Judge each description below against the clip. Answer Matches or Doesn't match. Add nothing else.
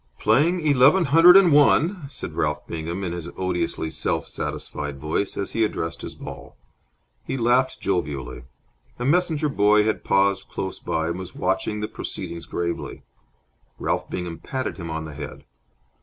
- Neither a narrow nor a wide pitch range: Doesn't match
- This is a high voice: Doesn't match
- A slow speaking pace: Doesn't match